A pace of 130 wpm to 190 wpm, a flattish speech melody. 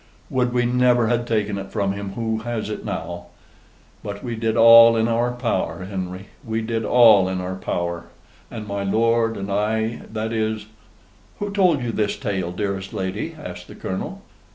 No: average, 180 wpm; average, 3.1 semitones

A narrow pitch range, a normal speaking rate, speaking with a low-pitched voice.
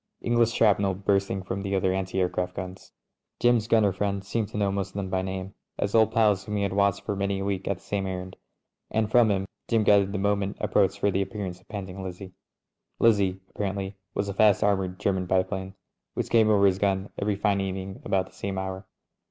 No: narrow, 1.4 semitones; fast, 220 wpm; low, 100 Hz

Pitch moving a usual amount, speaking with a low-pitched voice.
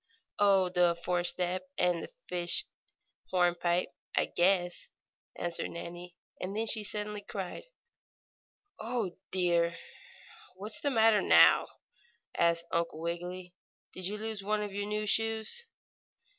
No: average, 3.2 semitones; medium, 185 Hz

